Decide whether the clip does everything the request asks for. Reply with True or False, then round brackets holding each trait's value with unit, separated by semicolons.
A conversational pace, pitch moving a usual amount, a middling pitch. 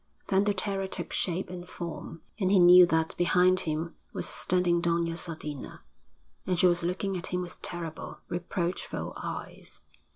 False (160 wpm; 1.4 semitones; 175 Hz)